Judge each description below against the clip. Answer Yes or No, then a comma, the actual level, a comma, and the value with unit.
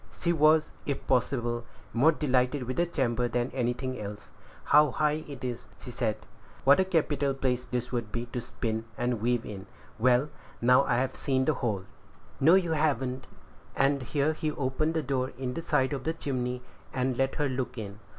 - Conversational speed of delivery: Yes, average, 185 wpm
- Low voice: Yes, low, 130 Hz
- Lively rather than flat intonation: No, average, 3.0 semitones